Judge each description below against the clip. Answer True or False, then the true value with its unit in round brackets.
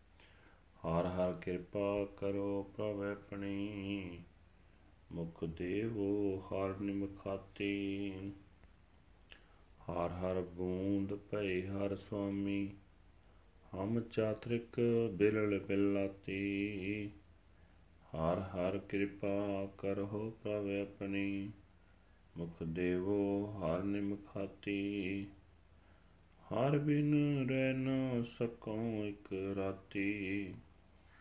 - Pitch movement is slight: True (2.2 semitones)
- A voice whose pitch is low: True (100 Hz)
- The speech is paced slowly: True (65 wpm)